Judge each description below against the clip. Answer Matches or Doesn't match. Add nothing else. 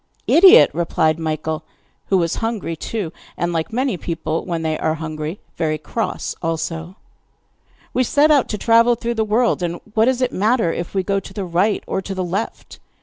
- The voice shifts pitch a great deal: Matches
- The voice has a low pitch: Doesn't match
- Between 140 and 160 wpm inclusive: Doesn't match